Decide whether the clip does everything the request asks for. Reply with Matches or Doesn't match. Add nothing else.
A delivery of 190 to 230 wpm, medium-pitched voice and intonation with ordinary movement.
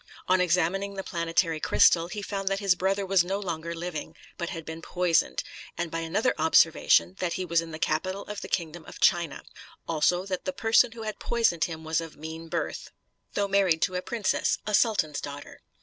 Matches